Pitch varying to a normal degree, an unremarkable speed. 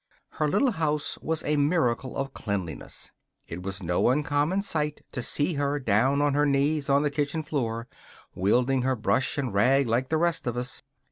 Yes: average, 3.6 semitones; average, 185 wpm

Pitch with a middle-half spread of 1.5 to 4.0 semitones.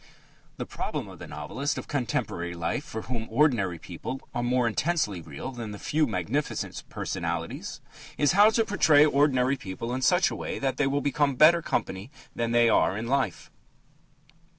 No: average, 5.3 semitones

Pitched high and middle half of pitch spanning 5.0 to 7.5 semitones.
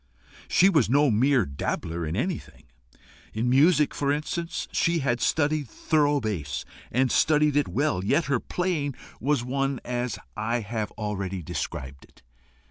No: low, 130 Hz; wide, 5.6 semitones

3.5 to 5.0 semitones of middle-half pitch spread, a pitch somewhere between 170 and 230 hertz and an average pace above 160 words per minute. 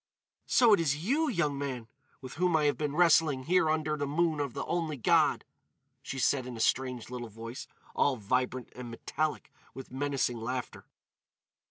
No: average, 3.8 semitones; medium, 140 Hz; average, 175 wpm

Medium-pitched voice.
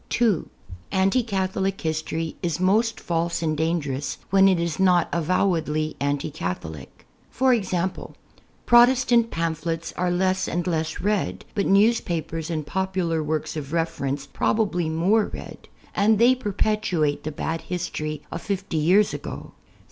Yes: medium, 175 Hz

